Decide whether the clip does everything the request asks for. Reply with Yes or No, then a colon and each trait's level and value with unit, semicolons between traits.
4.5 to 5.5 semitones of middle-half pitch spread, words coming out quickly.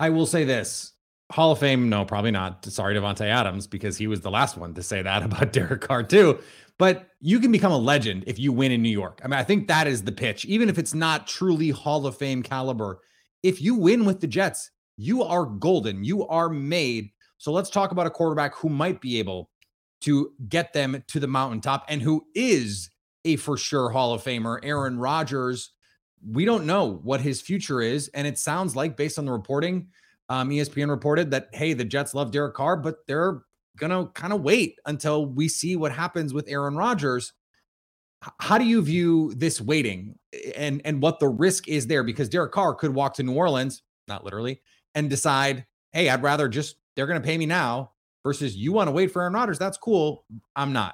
Yes: average, 4.8 semitones; fast, 210 wpm